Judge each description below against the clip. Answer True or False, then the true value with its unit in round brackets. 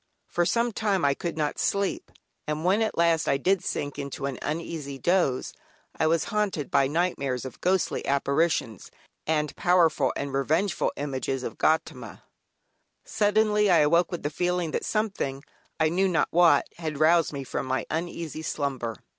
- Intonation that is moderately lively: True (4.2 semitones)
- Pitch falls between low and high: True (160 Hz)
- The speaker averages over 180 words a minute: False (165 wpm)